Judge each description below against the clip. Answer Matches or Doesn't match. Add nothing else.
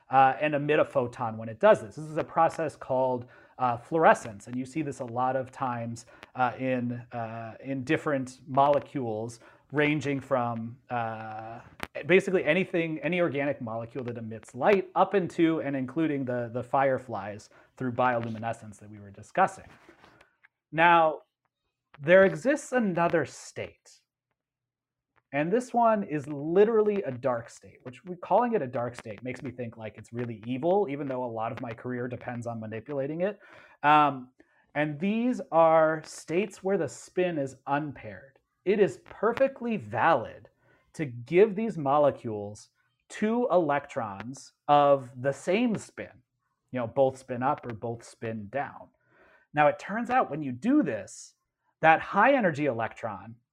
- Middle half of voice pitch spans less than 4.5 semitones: Doesn't match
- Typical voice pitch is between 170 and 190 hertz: Doesn't match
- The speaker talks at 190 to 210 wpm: Doesn't match